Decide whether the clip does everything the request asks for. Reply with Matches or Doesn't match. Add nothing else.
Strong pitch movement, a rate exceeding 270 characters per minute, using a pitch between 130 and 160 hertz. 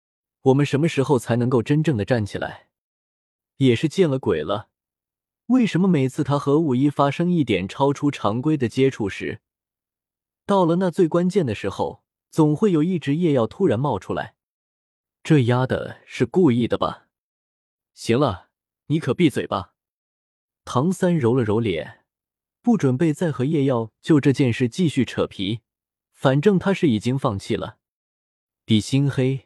Doesn't match